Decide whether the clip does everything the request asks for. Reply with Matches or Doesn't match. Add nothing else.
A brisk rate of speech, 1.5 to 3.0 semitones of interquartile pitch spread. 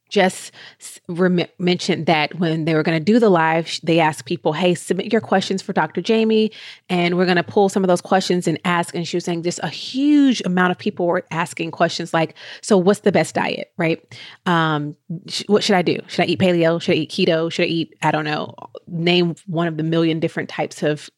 Matches